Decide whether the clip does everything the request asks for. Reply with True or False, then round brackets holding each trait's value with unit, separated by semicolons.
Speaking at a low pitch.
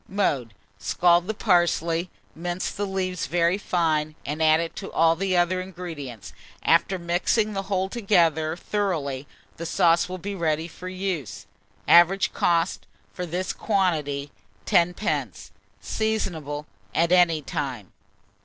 False (175 Hz)